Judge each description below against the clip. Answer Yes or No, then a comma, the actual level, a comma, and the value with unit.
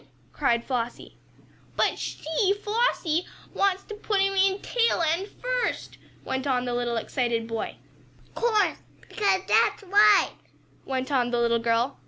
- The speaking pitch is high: Yes, very high, 325 Hz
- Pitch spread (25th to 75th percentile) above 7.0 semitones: Yes, wide, 8.9 semitones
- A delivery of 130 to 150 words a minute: Yes, average, 145 wpm